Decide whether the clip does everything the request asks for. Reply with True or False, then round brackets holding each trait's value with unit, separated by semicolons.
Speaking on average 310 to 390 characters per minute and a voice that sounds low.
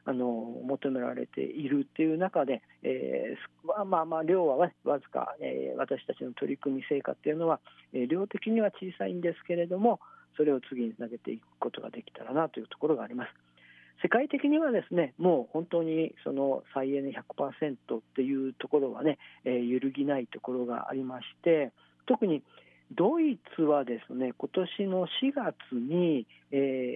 False (330 characters per minute; 150 Hz)